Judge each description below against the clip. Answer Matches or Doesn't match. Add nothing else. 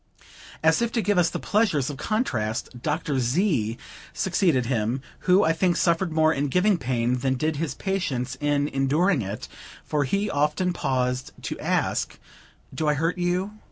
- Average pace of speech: Matches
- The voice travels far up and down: Matches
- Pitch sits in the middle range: Matches